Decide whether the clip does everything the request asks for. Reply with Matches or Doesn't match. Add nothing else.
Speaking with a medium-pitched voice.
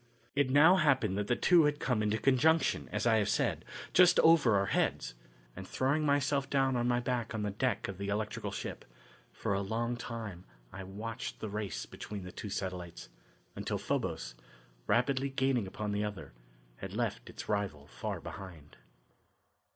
Doesn't match